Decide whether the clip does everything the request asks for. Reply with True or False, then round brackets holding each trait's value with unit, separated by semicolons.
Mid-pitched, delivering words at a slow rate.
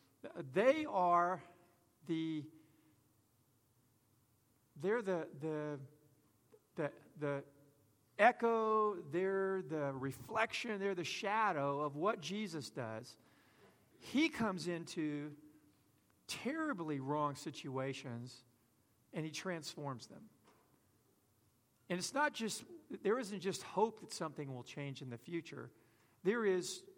True (150 Hz; 100 wpm)